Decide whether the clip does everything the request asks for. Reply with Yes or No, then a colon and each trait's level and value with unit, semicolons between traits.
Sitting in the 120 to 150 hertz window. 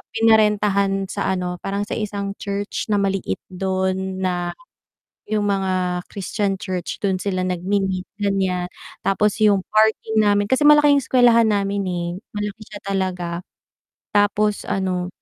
No: high, 195 Hz